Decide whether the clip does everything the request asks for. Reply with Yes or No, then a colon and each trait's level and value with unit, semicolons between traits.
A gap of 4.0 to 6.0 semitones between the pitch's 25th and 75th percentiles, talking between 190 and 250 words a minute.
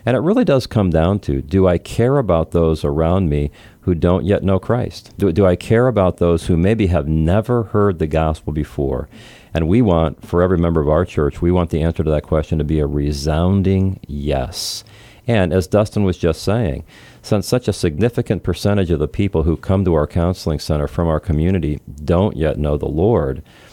Yes: average, 4.4 semitones; fast, 205 wpm